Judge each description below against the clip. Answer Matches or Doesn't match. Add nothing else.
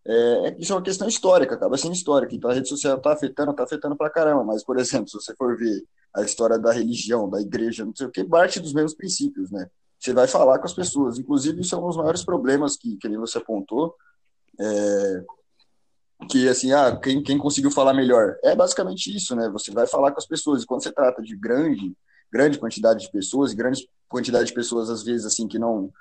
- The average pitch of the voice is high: Doesn't match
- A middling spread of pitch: Doesn't match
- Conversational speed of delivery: Doesn't match